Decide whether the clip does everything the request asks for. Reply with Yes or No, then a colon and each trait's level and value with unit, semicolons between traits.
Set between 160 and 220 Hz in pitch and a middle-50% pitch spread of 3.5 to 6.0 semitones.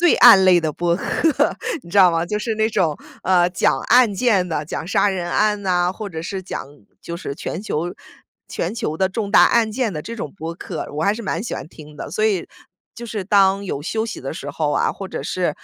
Yes: high, 190 Hz; average, 4.0 semitones